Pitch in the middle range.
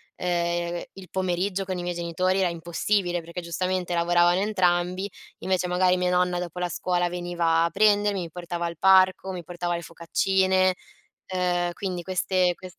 Yes: medium, 180 Hz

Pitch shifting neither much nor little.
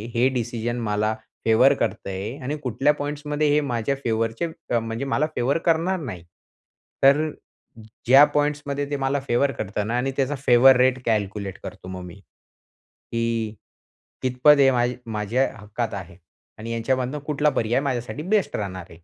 Yes: average, 4.2 semitones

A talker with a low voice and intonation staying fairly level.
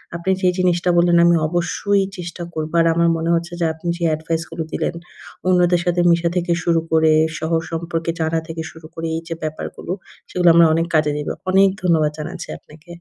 No: medium, 170 Hz; narrow, 1.4 semitones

